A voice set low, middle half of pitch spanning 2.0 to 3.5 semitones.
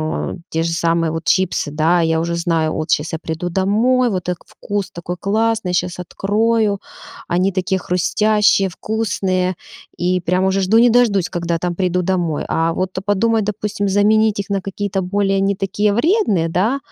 No: high, 190 Hz; average, 3.2 semitones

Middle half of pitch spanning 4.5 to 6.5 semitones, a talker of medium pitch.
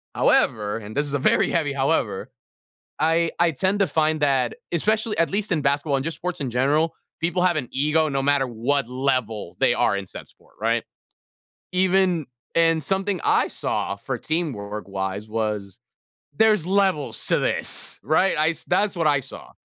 Yes: average, 5.2 semitones; medium, 150 Hz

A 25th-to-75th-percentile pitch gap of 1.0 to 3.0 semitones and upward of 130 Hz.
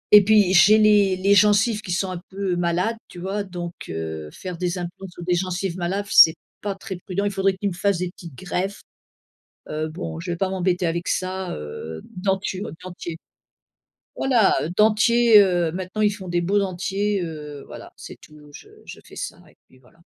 Yes: narrow, 2.6 semitones; medium, 185 Hz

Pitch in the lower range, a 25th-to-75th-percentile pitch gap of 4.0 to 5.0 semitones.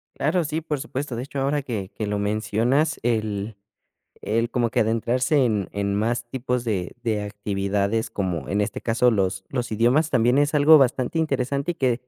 Yes: low, 120 Hz; average, 4.7 semitones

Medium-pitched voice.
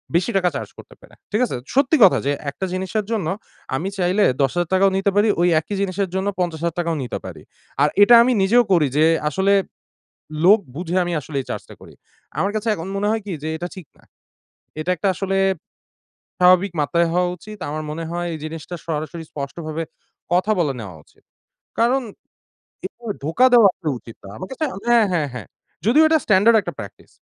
Yes: medium, 180 Hz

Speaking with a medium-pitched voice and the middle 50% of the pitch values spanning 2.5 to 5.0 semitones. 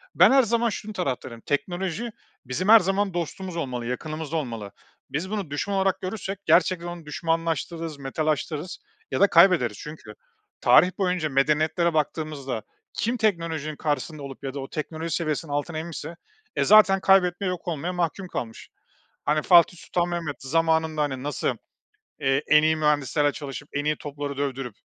Yes: medium, 160 Hz; average, 3.8 semitones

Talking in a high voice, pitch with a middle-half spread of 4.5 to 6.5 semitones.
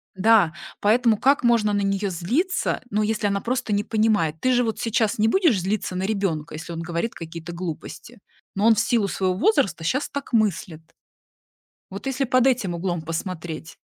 Yes: high, 205 Hz; average, 4.9 semitones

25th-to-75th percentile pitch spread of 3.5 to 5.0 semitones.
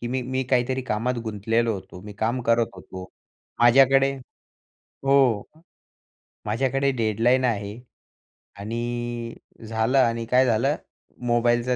No: narrow, 2.5 semitones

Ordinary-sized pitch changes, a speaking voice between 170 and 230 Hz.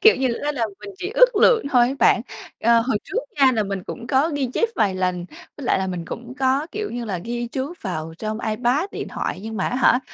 No: average, 4.6 semitones; high, 240 Hz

